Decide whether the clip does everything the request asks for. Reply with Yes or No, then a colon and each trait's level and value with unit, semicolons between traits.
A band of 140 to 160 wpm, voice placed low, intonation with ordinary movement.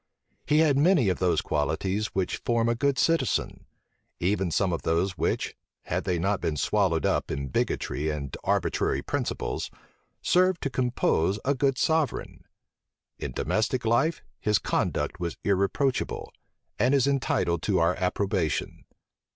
No: average, 145 wpm; low, 105 Hz; wide, 7.7 semitones